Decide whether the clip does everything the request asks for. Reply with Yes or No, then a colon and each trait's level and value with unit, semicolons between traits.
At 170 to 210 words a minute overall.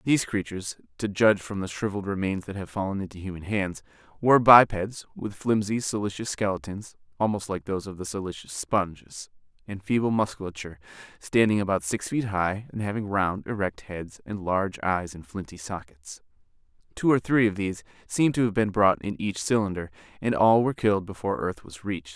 Yes: average, 180 wpm